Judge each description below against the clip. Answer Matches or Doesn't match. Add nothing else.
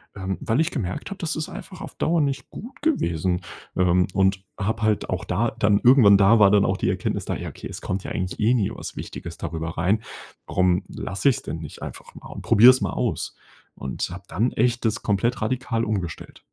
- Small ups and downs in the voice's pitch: Doesn't match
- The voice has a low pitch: Matches